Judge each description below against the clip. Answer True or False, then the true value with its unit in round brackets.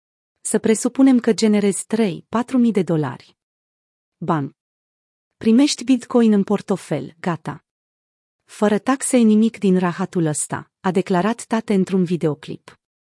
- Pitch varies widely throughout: True (5.7 semitones)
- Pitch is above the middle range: True (200 Hz)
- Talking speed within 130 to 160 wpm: False (115 wpm)